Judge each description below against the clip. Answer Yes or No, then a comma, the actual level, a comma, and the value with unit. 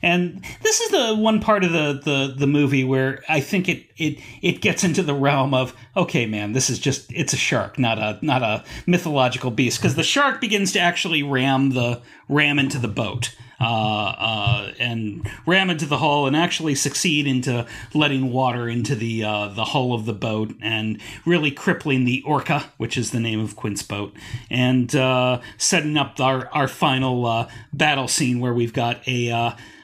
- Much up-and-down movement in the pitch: No, average, 4.3 semitones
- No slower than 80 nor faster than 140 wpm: No, average, 195 wpm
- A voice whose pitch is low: Yes, low, 130 Hz